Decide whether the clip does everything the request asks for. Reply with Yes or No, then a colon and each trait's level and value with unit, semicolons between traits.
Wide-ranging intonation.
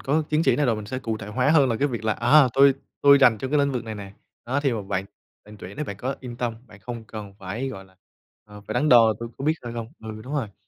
No: average, 4.2 semitones